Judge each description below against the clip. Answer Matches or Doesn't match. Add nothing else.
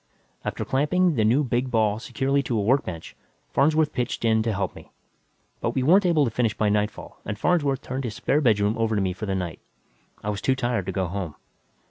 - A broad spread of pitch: Doesn't match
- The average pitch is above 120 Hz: Doesn't match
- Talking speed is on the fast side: Matches